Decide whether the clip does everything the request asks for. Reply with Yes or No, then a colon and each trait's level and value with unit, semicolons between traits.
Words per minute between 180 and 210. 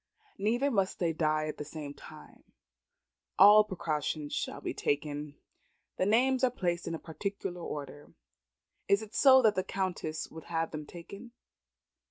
No: average, 150 wpm